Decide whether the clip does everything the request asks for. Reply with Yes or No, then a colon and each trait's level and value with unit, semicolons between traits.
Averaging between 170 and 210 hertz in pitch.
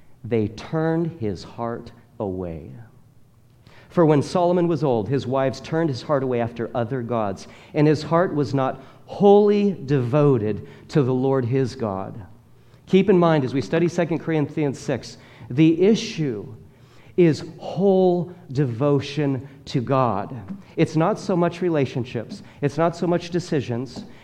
No: medium, 140 Hz